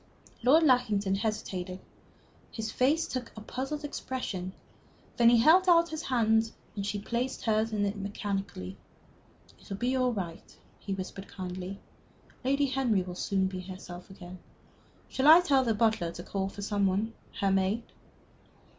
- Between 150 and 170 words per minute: Yes, average, 155 wpm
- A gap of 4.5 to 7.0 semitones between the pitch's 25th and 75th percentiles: Yes, average, 4.8 semitones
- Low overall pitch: No, high, 215 Hz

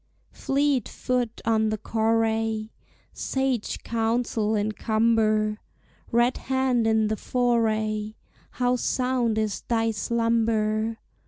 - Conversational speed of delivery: No, slow, 100 wpm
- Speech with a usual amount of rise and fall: No, narrow, 1.9 semitones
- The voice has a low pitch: No, high, 225 Hz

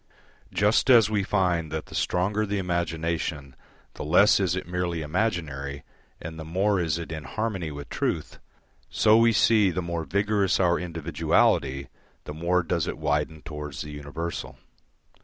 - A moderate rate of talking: Yes, average, 160 wpm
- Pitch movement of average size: Yes, average, 3.8 semitones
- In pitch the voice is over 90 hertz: No, very low, 85 Hz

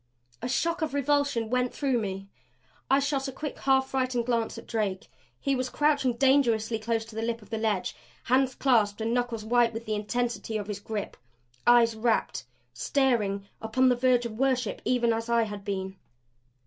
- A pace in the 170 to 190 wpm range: Yes, average, 185 wpm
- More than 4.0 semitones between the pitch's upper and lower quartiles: No, average, 3.0 semitones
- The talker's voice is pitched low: No, high, 235 Hz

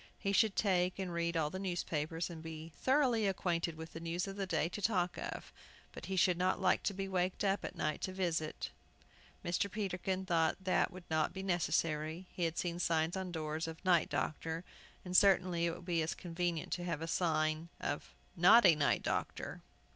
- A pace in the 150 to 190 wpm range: No, fast, 205 wpm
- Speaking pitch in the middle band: Yes, medium, 175 Hz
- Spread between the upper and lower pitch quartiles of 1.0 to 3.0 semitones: Yes, narrow, 2.5 semitones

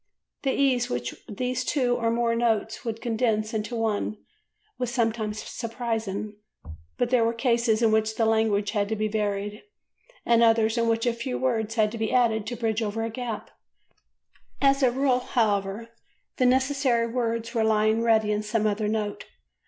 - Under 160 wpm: No, average, 175 wpm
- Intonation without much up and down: Yes, narrow, 1.9 semitones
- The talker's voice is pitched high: Yes, high, 225 Hz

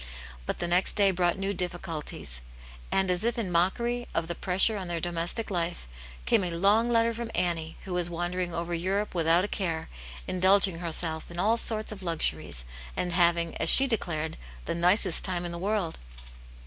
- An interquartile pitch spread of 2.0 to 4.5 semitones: Yes, average, 2.8 semitones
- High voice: No, medium, 175 Hz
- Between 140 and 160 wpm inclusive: No, average, 185 wpm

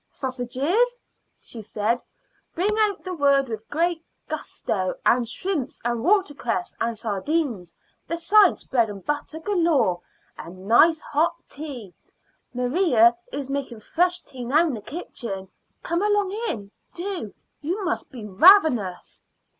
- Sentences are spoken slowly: Yes, slow, 130 wpm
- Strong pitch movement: Yes, wide, 7.2 semitones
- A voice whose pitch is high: Yes, very high, 275 Hz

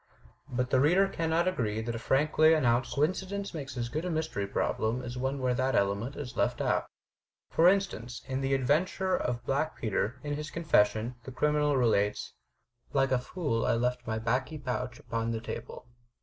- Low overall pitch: Yes, low, 130 Hz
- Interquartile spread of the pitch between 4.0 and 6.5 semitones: Yes, average, 4.6 semitones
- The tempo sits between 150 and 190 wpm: Yes, average, 180 wpm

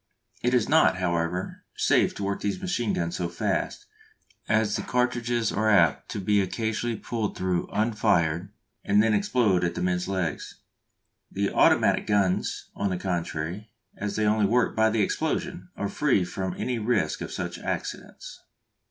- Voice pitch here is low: Yes, low, 100 Hz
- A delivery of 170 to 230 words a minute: No, average, 160 wpm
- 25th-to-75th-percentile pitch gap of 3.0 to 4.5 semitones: Yes, average, 3.6 semitones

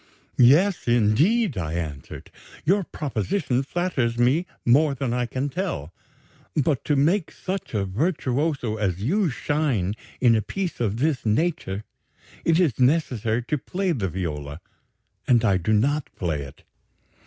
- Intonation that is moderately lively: No, wide, 7.0 semitones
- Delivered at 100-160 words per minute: Yes, average, 145 wpm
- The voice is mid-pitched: No, low, 125 Hz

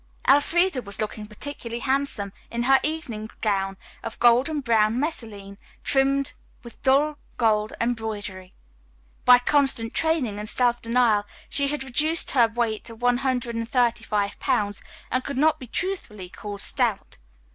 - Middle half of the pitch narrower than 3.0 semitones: No, average, 4.2 semitones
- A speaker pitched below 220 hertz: No, high, 240 Hz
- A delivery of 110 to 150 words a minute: Yes, average, 145 wpm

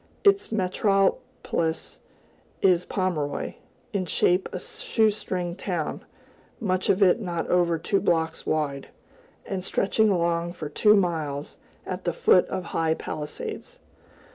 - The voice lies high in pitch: No, medium, 180 Hz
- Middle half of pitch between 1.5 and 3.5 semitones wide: Yes, average, 3.2 semitones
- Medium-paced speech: No, slow, 125 wpm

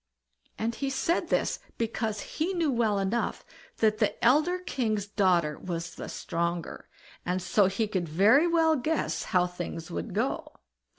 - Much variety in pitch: Yes, wide, 7.1 semitones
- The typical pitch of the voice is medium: No, high, 215 Hz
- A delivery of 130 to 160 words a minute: Yes, average, 155 wpm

